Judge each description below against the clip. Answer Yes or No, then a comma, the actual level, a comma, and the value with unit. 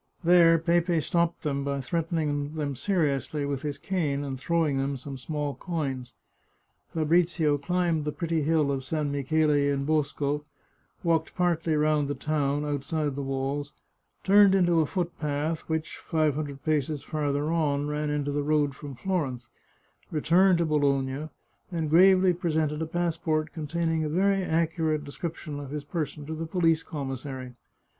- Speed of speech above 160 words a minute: No, average, 155 wpm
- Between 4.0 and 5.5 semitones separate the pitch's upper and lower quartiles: No, narrow, 2.6 semitones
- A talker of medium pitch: Yes, medium, 155 Hz